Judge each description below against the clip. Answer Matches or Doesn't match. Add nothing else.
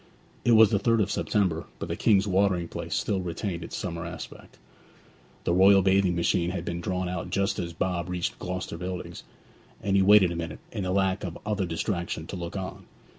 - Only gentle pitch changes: Matches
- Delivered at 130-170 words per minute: Doesn't match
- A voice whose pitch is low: Matches